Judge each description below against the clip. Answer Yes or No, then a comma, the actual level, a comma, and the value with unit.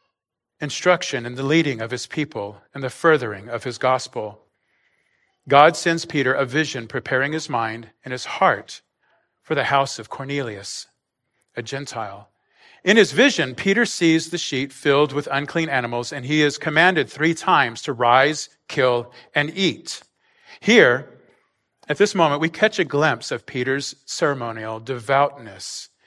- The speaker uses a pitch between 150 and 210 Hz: No, medium, 140 Hz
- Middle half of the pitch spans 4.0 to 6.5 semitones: Yes, average, 4.3 semitones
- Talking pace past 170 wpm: No, average, 150 wpm